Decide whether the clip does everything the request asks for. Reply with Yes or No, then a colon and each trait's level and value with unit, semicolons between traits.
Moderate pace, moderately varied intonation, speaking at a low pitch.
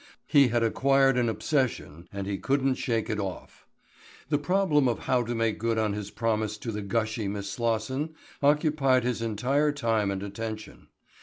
Yes: average, 170 wpm; average, 4.2 semitones; low, 115 Hz